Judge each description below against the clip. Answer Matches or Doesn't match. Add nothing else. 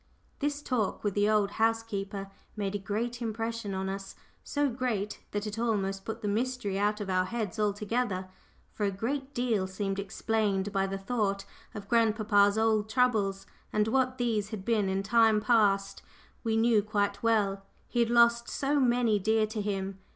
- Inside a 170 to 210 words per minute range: Matches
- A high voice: Matches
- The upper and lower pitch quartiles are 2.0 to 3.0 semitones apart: Matches